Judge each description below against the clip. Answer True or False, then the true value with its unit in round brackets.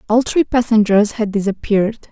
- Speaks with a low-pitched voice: False (220 Hz)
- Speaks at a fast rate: False (140 wpm)